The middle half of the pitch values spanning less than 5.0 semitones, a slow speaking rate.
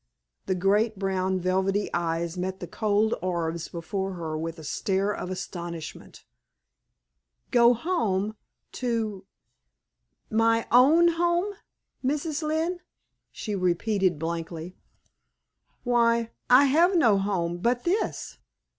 No: average, 5.3 semitones; slow, 110 wpm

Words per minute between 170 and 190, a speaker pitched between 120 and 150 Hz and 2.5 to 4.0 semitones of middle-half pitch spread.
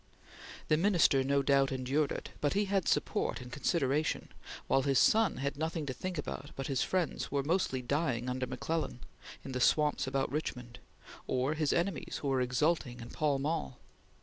Yes: average, 180 wpm; medium, 140 Hz; average, 3.4 semitones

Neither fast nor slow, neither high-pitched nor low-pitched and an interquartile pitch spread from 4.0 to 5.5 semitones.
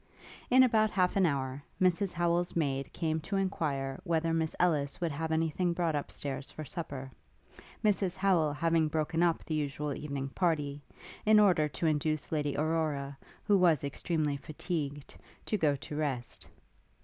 No: average, 160 wpm; medium, 160 Hz; average, 3.4 semitones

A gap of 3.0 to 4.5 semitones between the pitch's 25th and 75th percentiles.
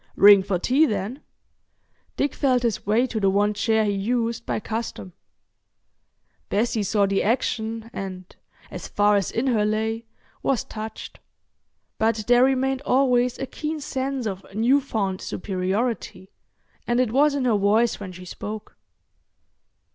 Yes: average, 3.6 semitones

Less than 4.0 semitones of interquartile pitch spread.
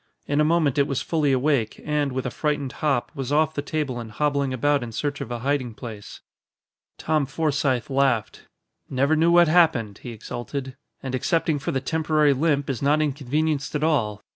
Yes: average, 2.9 semitones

